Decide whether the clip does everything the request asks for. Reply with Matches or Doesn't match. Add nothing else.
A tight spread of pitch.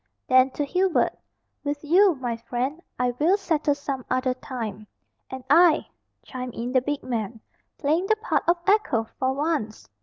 Doesn't match